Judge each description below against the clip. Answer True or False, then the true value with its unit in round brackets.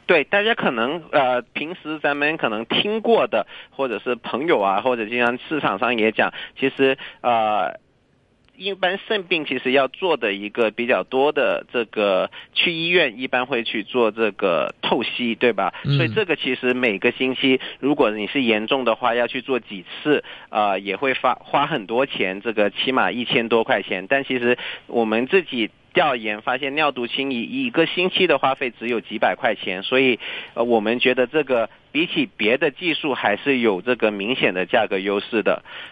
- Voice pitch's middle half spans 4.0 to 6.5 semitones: False (3.6 semitones)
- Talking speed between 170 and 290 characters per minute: True (265 characters per minute)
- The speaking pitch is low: True (125 Hz)